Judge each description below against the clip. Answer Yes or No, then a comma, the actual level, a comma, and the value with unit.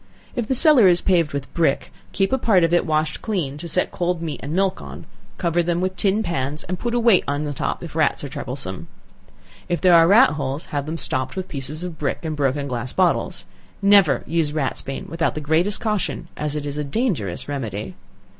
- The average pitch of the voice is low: No, medium, 165 Hz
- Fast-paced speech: Yes, fast, 215 wpm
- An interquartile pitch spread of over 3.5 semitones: Yes, average, 4.5 semitones